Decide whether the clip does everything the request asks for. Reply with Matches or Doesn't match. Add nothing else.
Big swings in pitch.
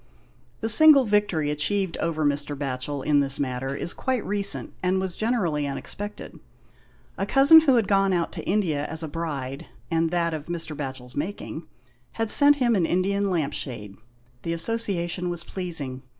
Matches